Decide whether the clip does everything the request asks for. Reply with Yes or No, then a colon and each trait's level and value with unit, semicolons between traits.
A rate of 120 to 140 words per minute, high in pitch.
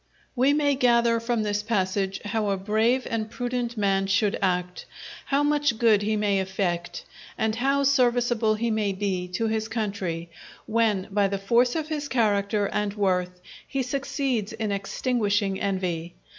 No: average, 155 wpm; high, 215 Hz